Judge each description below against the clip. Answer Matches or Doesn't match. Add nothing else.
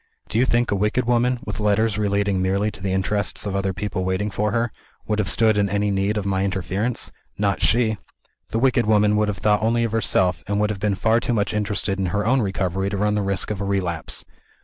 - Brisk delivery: Matches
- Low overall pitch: Matches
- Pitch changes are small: Matches